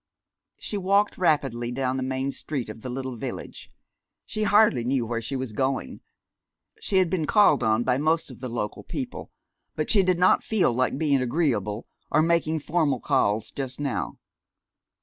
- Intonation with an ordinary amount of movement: No, wide, 5.7 semitones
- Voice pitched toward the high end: No, low, 135 Hz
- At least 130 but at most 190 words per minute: Yes, average, 170 wpm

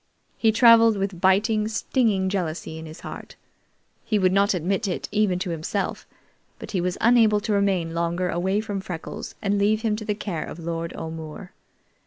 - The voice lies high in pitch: Yes, high, 195 Hz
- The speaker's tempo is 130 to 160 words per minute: No, average, 180 wpm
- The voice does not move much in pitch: No, average, 3.6 semitones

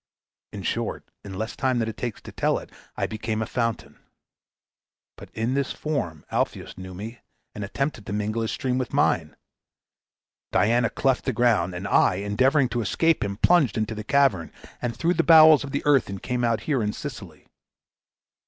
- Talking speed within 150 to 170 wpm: No, average, 180 wpm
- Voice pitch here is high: No, low, 115 Hz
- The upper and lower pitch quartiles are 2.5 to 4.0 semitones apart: No, average, 4.5 semitones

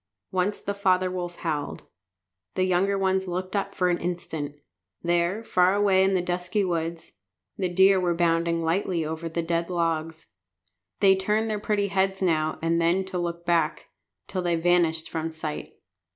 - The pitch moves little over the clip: Yes, narrow, 2.3 semitones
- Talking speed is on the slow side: No, average, 165 wpm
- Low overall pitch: No, medium, 175 Hz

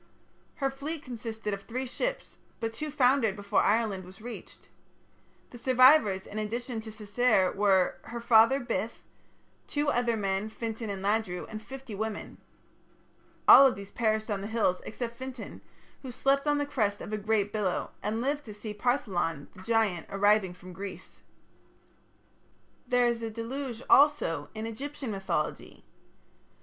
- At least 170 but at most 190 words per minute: No, average, 155 wpm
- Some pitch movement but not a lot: Yes, average, 3.7 semitones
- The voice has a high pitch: Yes, high, 225 Hz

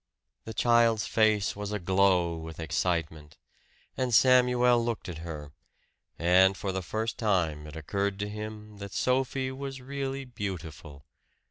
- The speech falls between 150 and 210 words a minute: No, slow, 135 wpm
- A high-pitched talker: No, low, 100 Hz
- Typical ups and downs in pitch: No, wide, 5.7 semitones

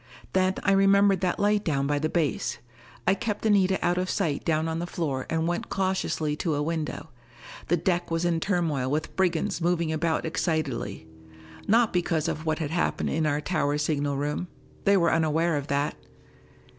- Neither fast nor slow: Yes, average, 180 wpm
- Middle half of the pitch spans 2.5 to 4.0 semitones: Yes, average, 3.6 semitones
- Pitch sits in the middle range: Yes, medium, 165 Hz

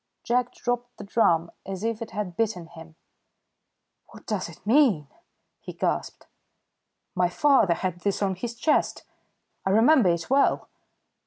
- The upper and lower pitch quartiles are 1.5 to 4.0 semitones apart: No, average, 5.3 semitones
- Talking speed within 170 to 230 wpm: No, average, 145 wpm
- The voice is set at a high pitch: Yes, high, 205 Hz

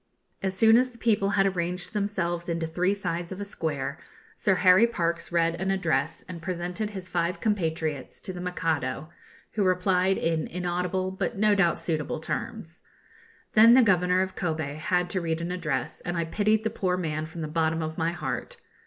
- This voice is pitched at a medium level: Yes, medium, 180 Hz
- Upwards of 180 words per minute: Yes, average, 190 wpm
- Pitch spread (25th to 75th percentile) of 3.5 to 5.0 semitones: No, average, 2.7 semitones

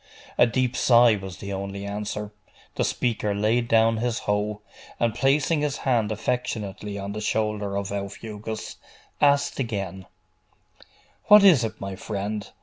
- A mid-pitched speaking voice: No, low, 105 Hz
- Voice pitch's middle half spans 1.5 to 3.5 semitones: Yes, average, 3.2 semitones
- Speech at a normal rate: Yes, average, 145 wpm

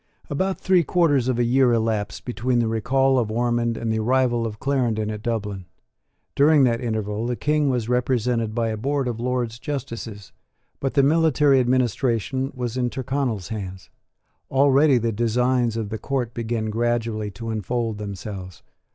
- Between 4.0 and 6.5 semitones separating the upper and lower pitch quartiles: No, average, 3.0 semitones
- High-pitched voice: No, low, 120 Hz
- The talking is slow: No, average, 160 wpm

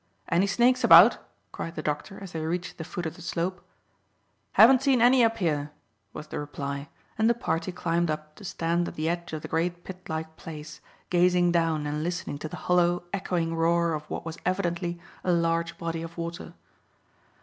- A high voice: No, medium, 170 Hz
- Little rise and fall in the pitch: Yes, narrow, 2.1 semitones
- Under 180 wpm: No, average, 195 wpm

